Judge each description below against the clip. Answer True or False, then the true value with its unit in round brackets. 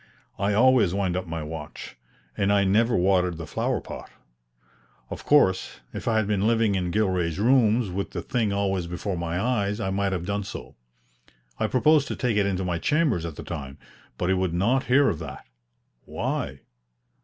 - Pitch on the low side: True (100 Hz)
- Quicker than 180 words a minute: True (190 wpm)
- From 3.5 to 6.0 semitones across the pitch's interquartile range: True (3.9 semitones)